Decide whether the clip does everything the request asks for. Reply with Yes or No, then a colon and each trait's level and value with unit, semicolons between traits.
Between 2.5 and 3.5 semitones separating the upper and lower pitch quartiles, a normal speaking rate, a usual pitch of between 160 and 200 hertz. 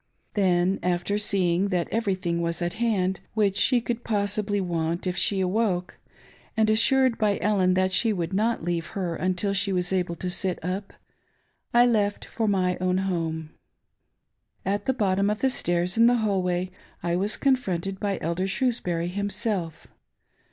Yes: average, 2.9 semitones; average, 170 wpm; high, 190 Hz